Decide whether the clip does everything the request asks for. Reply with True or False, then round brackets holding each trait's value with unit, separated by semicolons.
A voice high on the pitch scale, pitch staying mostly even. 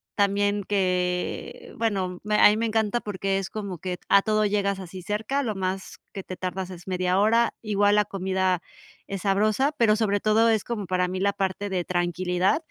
True (200 Hz; 2.3 semitones)